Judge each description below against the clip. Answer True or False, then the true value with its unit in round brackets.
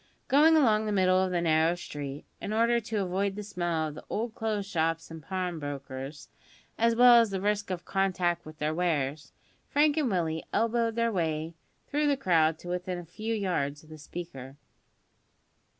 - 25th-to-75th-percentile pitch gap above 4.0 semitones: True (5.4 semitones)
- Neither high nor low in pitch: True (180 Hz)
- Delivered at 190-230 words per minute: False (180 wpm)